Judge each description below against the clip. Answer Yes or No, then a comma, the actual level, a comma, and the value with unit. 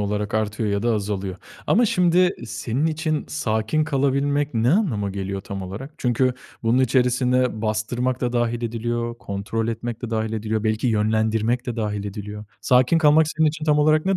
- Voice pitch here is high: No, low, 120 Hz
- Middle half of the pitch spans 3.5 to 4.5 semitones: Yes, average, 4.2 semitones